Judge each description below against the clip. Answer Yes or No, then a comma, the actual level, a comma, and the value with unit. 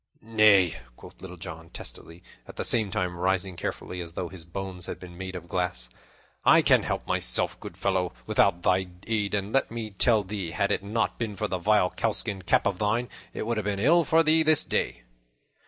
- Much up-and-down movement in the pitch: No, average, 3.3 semitones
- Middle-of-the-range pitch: No, very low, 95 Hz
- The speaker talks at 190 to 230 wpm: Yes, fast, 205 wpm